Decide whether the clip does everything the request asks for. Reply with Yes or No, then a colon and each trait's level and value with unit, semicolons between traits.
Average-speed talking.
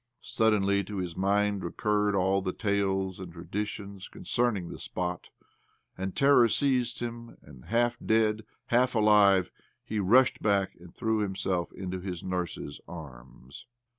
Yes: average, 145 wpm